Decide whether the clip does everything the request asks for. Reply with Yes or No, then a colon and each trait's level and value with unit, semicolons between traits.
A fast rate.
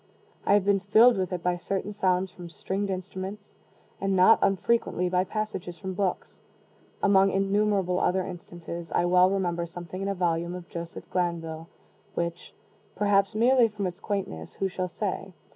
No: average, 160 wpm